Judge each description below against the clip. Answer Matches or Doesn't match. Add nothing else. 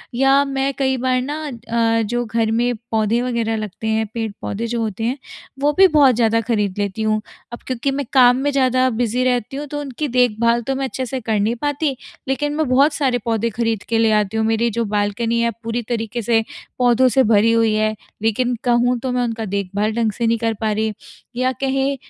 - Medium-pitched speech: Doesn't match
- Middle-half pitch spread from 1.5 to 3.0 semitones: Matches